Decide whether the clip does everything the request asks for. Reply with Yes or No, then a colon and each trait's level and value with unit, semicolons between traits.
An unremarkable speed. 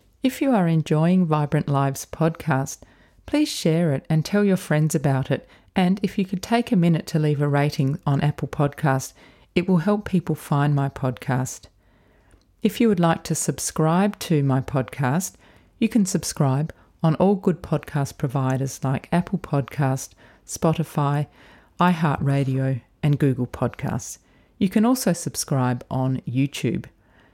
Yes: average, 150 wpm